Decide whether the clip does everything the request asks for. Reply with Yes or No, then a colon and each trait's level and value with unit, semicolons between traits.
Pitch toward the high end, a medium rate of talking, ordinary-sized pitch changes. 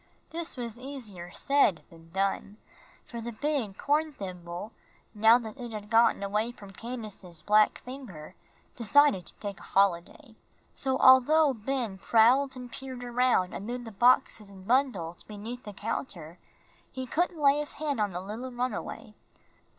Yes: high, 230 Hz; average, 150 wpm; average, 4.7 semitones